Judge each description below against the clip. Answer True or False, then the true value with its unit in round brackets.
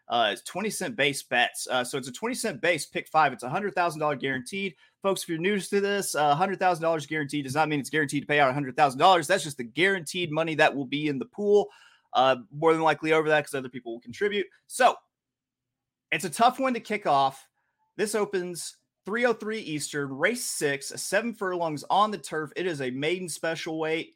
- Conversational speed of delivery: False (230 wpm)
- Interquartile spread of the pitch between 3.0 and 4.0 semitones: False (5.4 semitones)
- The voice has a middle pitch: True (160 Hz)